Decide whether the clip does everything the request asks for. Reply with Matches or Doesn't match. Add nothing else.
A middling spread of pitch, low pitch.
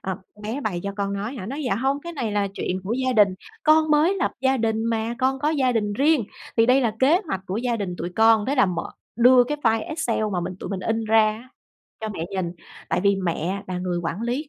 Doesn't match